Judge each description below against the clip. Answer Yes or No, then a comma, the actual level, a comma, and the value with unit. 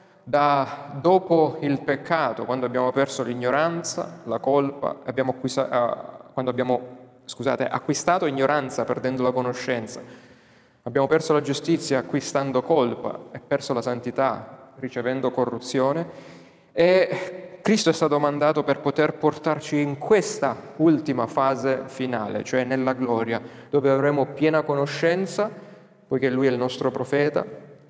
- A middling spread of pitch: Yes, average, 3.0 semitones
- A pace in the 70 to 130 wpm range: Yes, average, 125 wpm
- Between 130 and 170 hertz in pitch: Yes, low, 135 Hz